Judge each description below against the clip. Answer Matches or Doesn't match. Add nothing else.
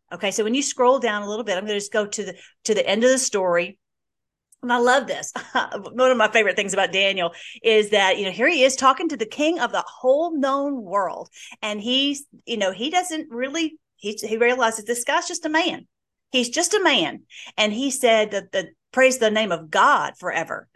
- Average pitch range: Matches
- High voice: Matches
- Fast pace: Matches